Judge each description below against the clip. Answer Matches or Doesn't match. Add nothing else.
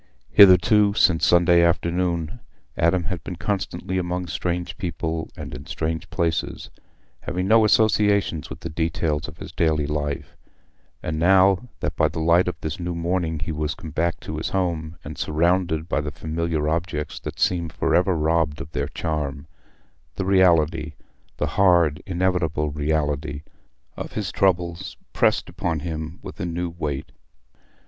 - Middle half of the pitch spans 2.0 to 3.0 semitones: Matches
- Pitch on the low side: Matches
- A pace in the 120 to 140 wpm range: Doesn't match